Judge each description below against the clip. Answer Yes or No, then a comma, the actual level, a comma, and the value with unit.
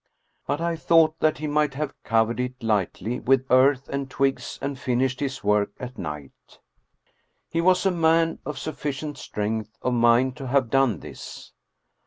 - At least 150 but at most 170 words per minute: Yes, average, 165 wpm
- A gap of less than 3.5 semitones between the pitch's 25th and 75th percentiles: No, average, 4.1 semitones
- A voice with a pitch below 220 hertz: Yes, low, 135 Hz